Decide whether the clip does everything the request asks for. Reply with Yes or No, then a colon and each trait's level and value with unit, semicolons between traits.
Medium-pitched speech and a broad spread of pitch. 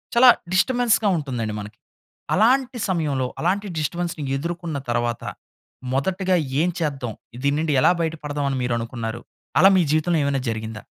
Yes: medium, 155 Hz; wide, 6.5 semitones